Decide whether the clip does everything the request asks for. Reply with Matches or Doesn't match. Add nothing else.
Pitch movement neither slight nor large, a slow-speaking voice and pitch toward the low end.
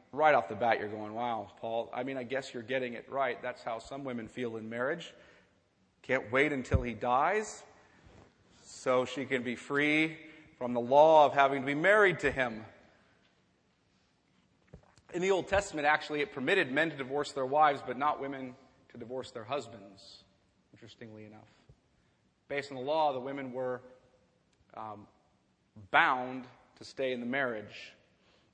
Doesn't match